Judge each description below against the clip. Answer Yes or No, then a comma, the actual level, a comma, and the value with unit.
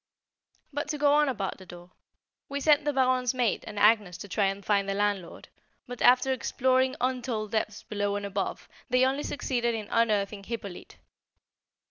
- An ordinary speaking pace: Yes, average, 170 wpm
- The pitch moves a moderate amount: Yes, average, 4.2 semitones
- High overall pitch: Yes, high, 230 Hz